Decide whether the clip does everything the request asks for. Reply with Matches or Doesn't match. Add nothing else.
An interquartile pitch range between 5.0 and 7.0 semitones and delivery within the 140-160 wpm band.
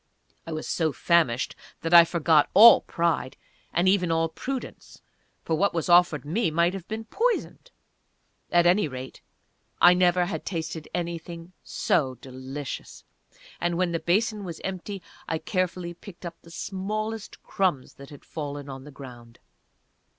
Doesn't match